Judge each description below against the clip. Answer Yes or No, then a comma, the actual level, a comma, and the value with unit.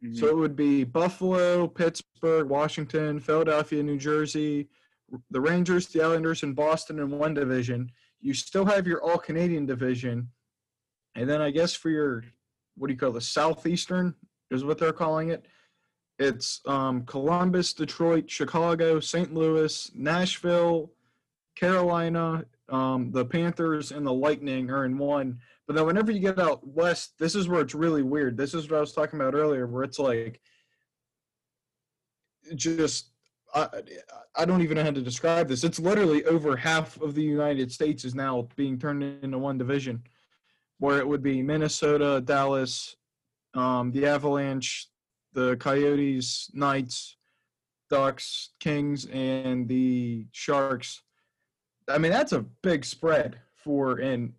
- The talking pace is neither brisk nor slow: Yes, average, 150 wpm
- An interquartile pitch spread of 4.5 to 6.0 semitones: No, average, 3.7 semitones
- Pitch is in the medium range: Yes, medium, 150 Hz